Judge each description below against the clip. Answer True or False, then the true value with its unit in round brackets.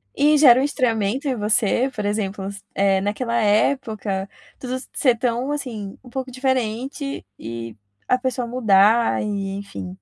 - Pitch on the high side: True (230 Hz)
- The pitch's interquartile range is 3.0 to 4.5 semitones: True (4.2 semitones)